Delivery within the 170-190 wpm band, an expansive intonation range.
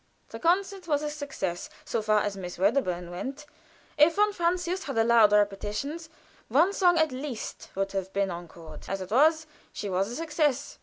Yes: average, 175 wpm; wide, 8.4 semitones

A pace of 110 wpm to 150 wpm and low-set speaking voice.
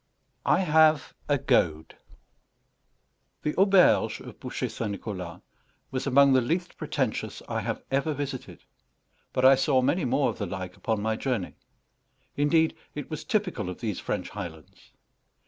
Yes: average, 145 wpm; low, 130 Hz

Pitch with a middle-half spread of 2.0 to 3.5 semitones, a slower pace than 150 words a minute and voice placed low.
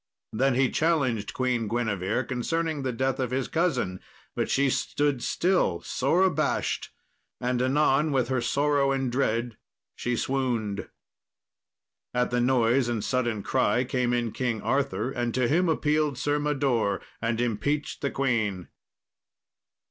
Yes: average, 3.0 semitones; average, 140 wpm; low, 130 Hz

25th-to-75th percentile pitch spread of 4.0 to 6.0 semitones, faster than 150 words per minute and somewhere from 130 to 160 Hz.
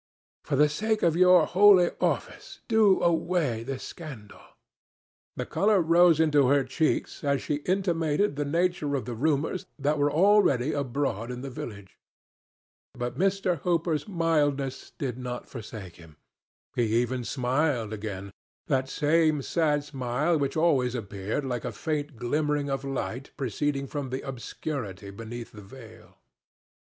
No: average, 4.8 semitones; average, 140 wpm; medium, 140 Hz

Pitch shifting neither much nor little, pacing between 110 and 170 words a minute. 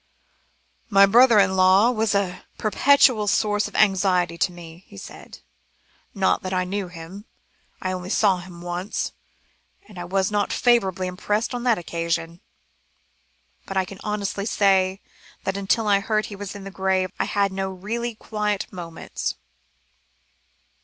No: narrow, 2.3 semitones; average, 155 wpm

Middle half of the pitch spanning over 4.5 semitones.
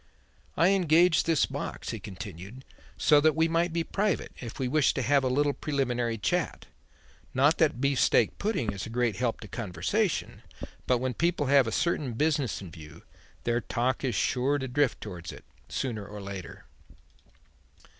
Yes: average, 5.2 semitones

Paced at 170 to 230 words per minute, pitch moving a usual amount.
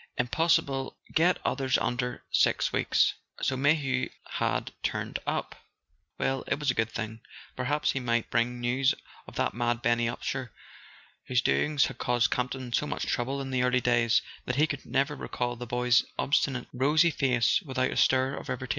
No: average, 175 wpm; narrow, 2.1 semitones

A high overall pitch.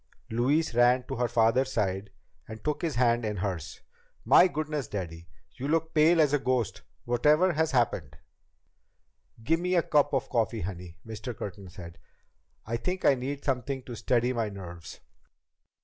No: low, 120 Hz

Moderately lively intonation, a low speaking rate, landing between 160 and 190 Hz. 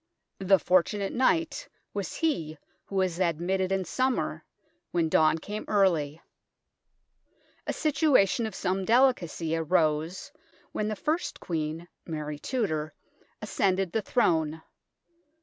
Yes: average, 5.0 semitones; slow, 115 wpm; medium, 185 Hz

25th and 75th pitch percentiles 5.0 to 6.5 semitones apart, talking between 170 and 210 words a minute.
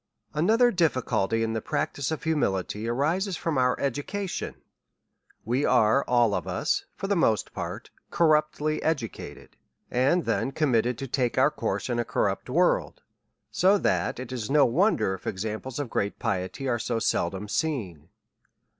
No: wide, 5.5 semitones; average, 155 wpm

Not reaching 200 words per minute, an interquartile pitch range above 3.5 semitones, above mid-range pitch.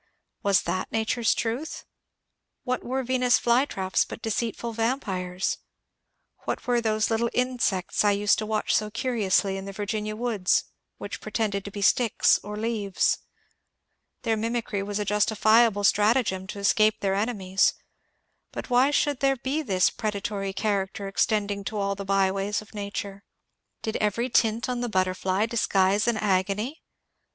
No: average, 150 wpm; average, 3.0 semitones; high, 210 Hz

